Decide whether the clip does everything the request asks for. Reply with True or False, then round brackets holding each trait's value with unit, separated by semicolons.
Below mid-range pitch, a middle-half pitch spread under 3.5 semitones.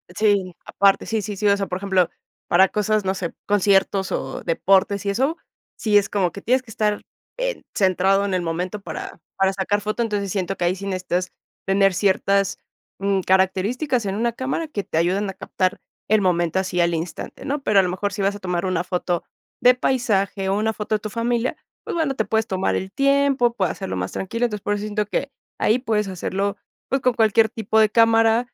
False (200 Hz; 2.9 semitones)